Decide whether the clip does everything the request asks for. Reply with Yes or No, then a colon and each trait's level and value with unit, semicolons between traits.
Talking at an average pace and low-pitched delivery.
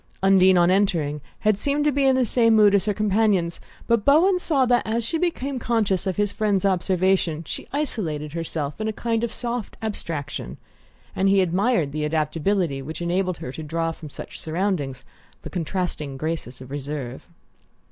No: average, 175 wpm; high, 190 Hz